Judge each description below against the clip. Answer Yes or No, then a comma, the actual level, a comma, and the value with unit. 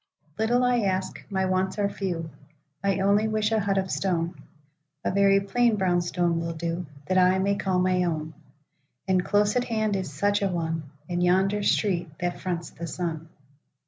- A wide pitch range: No, average, 3.3 semitones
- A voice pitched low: No, medium, 185 Hz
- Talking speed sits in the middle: Yes, average, 160 wpm